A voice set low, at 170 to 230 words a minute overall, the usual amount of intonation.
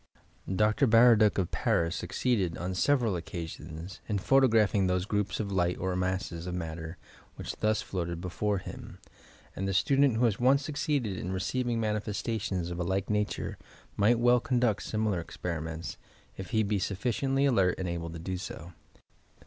No: low, 100 Hz; average, 160 wpm; average, 4.2 semitones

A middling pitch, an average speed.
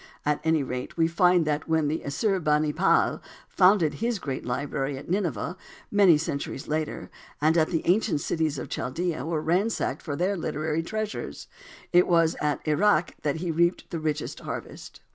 Yes: medium, 160 Hz; average, 160 wpm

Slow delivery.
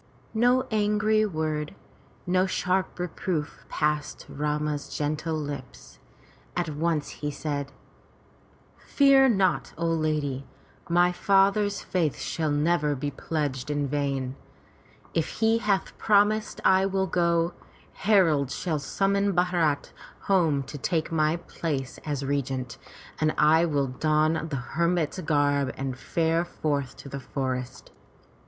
Yes: slow, 120 wpm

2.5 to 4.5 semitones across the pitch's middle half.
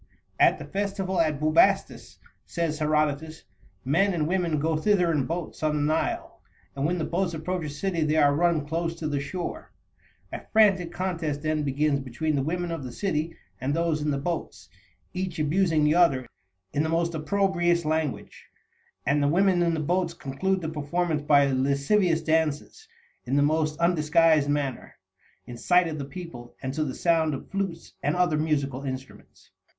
Yes: average, 3.0 semitones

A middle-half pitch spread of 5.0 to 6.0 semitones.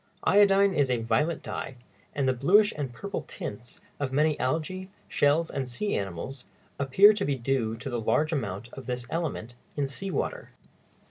Yes: wide, 5.6 semitones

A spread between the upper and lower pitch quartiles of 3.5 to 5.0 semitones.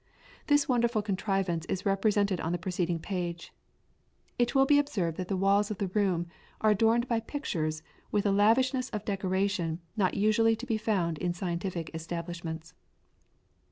Yes: average, 4.2 semitones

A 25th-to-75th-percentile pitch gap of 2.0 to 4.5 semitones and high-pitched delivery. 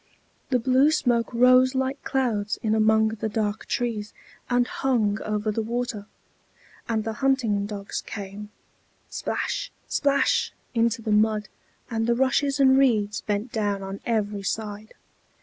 Yes: average, 3.2 semitones; high, 225 Hz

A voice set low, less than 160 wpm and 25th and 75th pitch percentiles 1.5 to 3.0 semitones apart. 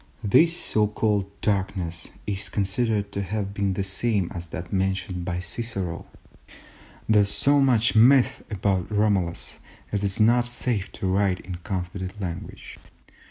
Yes: low, 100 Hz; average, 150 wpm; narrow, 2.6 semitones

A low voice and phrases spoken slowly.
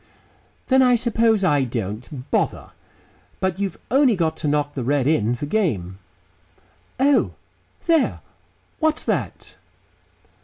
No: medium, 165 Hz; slow, 120 wpm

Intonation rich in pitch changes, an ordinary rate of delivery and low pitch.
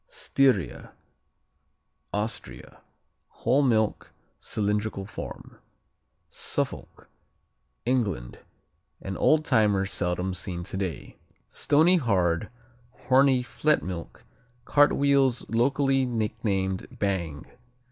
No: wide, 5.9 semitones; slow, 75 wpm; low, 110 Hz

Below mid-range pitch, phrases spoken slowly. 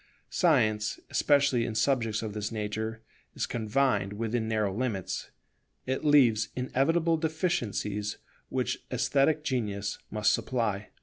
Yes: low, 115 Hz; slow, 115 wpm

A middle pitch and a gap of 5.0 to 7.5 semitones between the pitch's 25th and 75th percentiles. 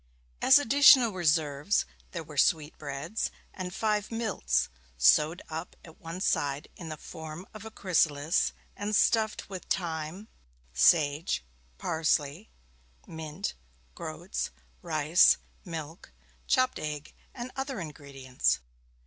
Yes: medium, 160 Hz; wide, 5.4 semitones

